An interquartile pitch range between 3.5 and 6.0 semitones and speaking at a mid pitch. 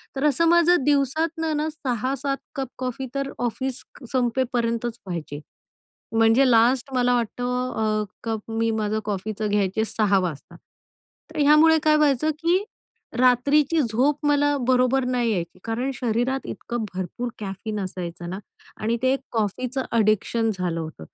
No: average, 4.1 semitones; high, 245 Hz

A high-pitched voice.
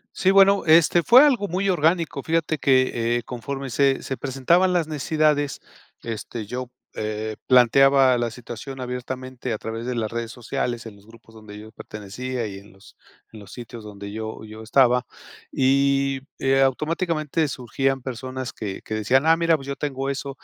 No: low, 130 Hz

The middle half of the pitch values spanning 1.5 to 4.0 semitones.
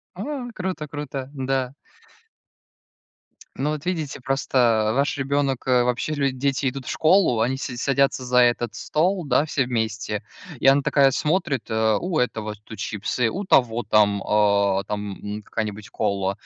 No: average, 4.5 semitones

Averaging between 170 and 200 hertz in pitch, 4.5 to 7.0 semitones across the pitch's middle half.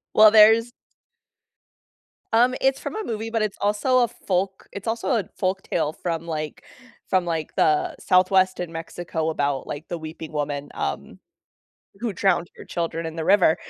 Yes: medium, 185 Hz; average, 5.0 semitones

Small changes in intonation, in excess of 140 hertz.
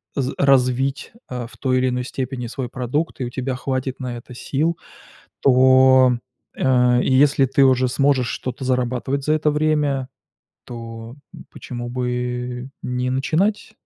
No: narrow, 1.6 semitones; low, 130 Hz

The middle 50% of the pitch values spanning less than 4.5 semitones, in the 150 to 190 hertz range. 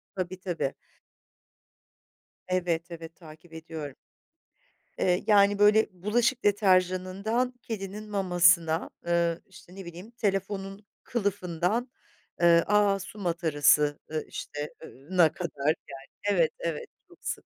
Yes: average, 3.4 semitones; medium, 185 Hz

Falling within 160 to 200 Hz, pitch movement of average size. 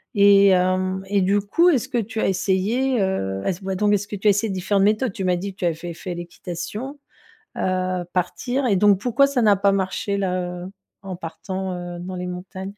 No: high, 190 Hz; narrow, 2.2 semitones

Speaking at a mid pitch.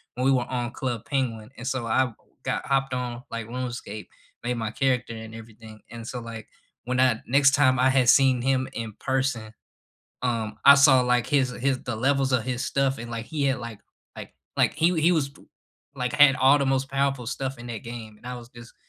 No: low, 125 Hz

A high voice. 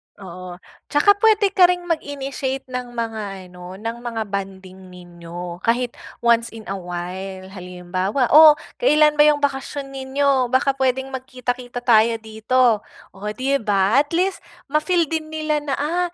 Yes: high, 245 Hz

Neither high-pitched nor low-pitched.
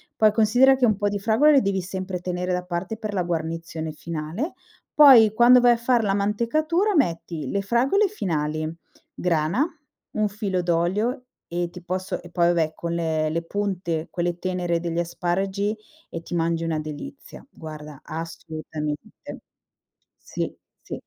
Yes: medium, 180 Hz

